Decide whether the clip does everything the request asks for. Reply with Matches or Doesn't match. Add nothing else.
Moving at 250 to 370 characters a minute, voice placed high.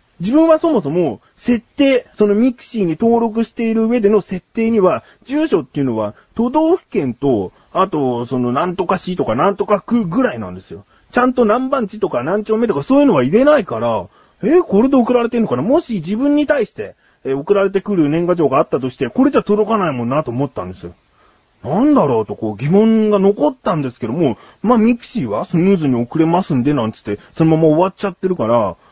Doesn't match